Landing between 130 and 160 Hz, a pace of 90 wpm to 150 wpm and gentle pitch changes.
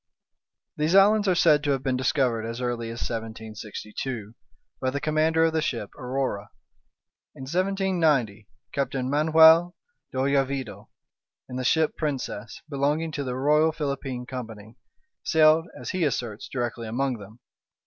No: low, 135 Hz; average, 140 wpm; average, 4.8 semitones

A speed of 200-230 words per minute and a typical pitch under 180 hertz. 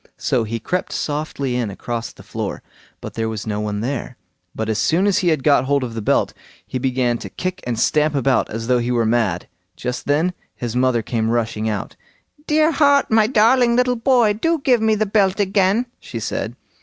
Yes: fast, 205 wpm; low, 135 Hz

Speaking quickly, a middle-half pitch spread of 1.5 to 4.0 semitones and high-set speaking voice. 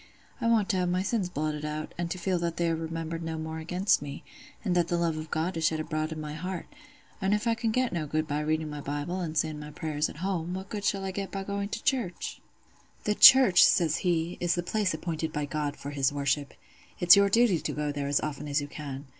No: fast, 255 wpm; average, 3.7 semitones; medium, 165 Hz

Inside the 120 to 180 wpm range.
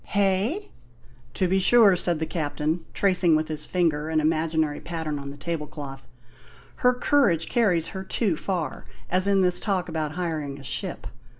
Yes: average, 170 wpm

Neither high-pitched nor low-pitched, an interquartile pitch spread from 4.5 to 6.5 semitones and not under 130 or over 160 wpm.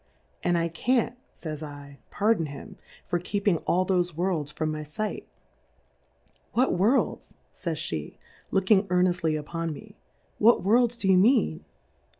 Yes: medium, 180 Hz; average, 4.9 semitones; average, 140 wpm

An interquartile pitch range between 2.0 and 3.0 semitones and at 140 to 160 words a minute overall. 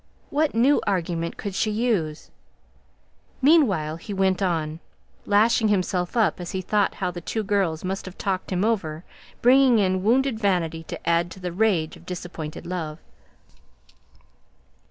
No: average, 4.2 semitones; average, 150 wpm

